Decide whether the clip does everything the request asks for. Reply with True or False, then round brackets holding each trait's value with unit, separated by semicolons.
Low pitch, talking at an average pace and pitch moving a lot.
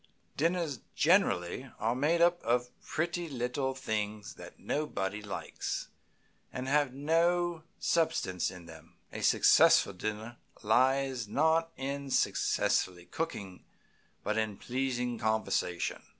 False (130 Hz; 110 wpm; 6.4 semitones)